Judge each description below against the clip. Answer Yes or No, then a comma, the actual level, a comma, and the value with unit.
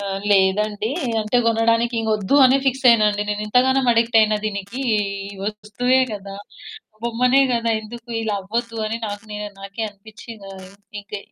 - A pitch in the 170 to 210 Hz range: No, high, 220 Hz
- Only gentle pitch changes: Yes, narrow, 2.3 semitones